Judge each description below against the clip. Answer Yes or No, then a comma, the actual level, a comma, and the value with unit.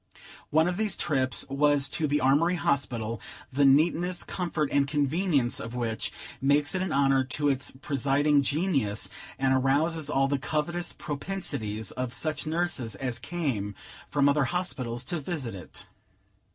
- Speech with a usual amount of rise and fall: Yes, average, 3.5 semitones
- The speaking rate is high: No, average, 150 wpm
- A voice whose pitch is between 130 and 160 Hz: Yes, medium, 140 Hz